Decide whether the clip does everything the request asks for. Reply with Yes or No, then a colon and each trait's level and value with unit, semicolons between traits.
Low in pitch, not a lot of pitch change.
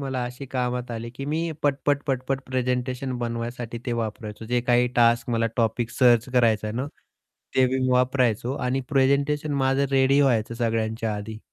Yes: low, 125 Hz; narrow, 2.2 semitones